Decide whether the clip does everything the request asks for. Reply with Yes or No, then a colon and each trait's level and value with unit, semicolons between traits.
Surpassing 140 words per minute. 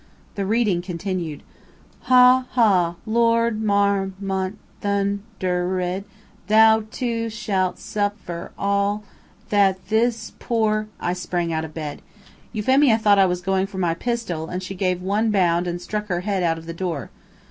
Yes: average, 160 wpm